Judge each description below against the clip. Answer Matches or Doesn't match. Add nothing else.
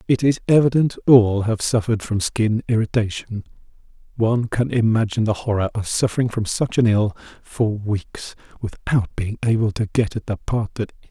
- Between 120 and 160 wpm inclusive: Doesn't match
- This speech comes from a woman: Doesn't match